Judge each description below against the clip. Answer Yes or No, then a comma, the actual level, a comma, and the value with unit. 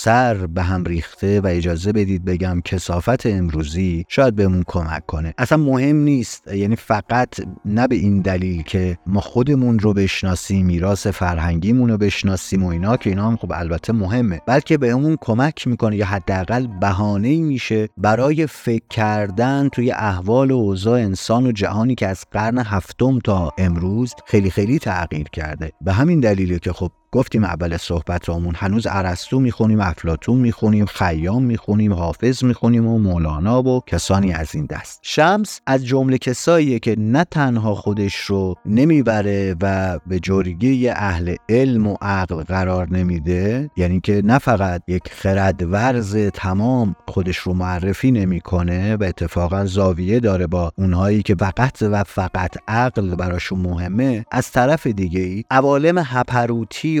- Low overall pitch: Yes, low, 100 Hz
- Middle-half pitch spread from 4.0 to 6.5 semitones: Yes, average, 4.9 semitones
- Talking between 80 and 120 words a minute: No, average, 150 wpm